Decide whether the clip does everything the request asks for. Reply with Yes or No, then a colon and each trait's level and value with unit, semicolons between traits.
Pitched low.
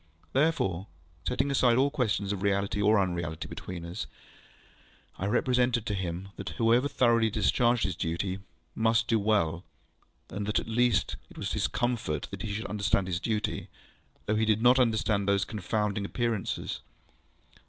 Yes: low, 105 Hz